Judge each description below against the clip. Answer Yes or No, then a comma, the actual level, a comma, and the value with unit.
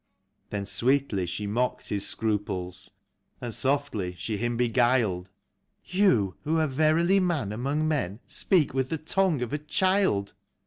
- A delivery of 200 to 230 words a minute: No, average, 145 wpm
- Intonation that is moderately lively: No, wide, 7.1 semitones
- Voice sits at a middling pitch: No, low, 125 Hz